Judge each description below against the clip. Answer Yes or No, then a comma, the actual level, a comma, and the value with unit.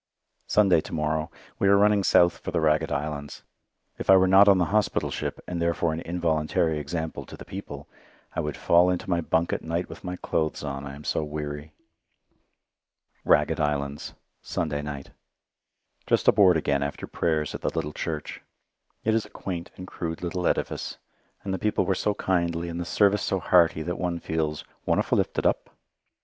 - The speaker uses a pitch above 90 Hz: No, very low, 85 Hz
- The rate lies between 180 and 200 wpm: Yes, average, 185 wpm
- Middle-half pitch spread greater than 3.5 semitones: No, average, 3.1 semitones